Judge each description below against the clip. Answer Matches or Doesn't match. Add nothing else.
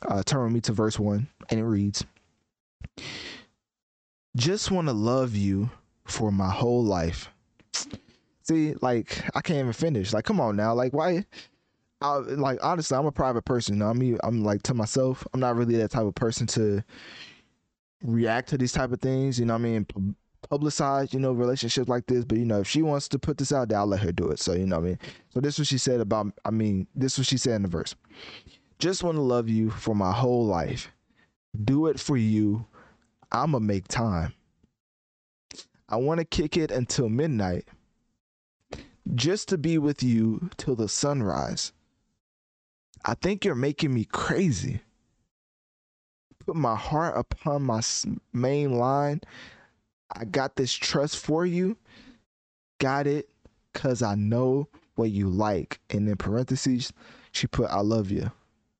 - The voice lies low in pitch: Matches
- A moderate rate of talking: Matches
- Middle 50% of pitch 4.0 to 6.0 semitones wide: Matches